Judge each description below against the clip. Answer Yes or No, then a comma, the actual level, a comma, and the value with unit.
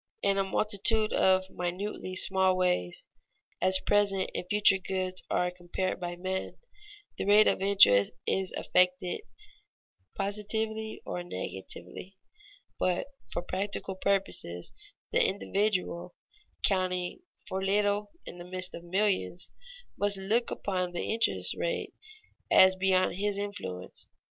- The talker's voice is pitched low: No, high, 190 Hz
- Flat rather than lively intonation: Yes, narrow, 2.0 semitones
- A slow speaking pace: Yes, slow, 120 wpm